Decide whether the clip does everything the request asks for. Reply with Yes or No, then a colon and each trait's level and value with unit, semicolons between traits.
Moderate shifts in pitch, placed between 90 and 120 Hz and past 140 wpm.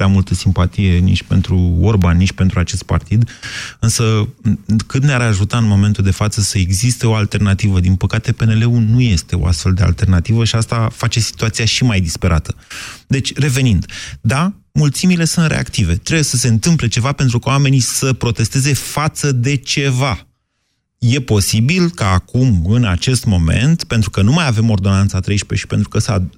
Yes: average, 4.5 semitones; low, 110 Hz; fast, 170 wpm